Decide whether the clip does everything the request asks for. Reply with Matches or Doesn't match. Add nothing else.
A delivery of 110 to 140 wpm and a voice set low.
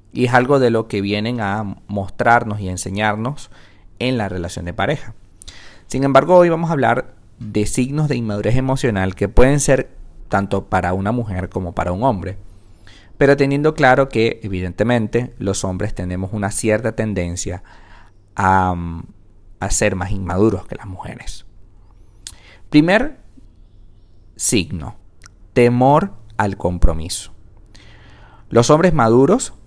Matches